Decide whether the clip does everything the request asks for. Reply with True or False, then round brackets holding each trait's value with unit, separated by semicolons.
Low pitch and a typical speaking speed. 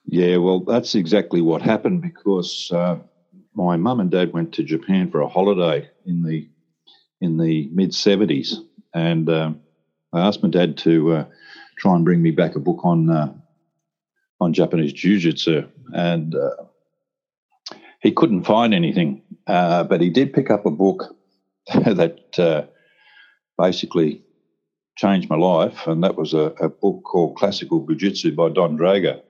True (90 Hz; 155 wpm)